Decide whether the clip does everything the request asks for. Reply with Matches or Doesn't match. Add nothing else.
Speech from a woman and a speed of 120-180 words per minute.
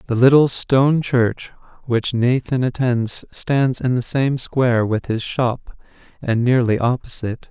Doesn't match